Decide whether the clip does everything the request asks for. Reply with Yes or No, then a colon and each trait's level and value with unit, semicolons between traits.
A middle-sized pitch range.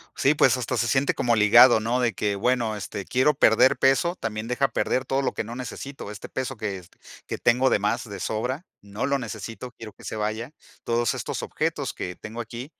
Yes: average, 3.2 semitones